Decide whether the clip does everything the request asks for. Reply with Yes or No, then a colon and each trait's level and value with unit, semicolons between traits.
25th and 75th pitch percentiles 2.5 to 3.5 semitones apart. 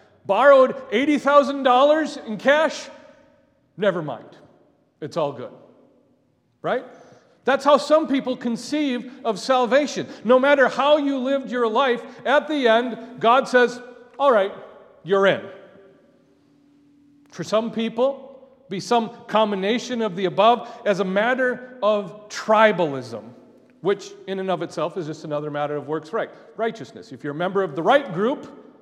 No: average, 5.3 semitones